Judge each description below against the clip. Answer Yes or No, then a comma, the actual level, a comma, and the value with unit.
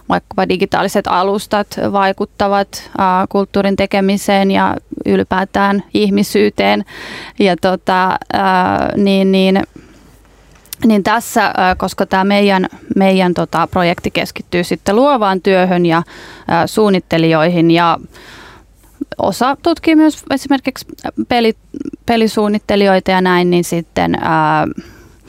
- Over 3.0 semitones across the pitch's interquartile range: No, average, 2.7 semitones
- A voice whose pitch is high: Yes, high, 195 Hz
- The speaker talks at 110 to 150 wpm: No, average, 100 wpm